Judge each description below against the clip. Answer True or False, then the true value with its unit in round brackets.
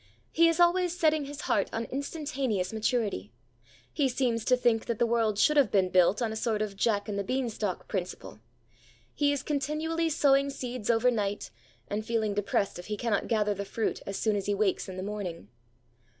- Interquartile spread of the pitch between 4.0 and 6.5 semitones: True (5.2 semitones)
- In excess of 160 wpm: True (195 wpm)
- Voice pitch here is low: False (225 Hz)